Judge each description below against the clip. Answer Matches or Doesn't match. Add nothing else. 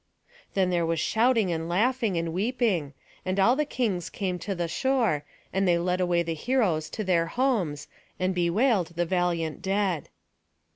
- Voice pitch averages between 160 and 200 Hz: Matches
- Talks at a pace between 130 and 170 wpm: Matches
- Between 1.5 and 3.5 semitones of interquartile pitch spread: Doesn't match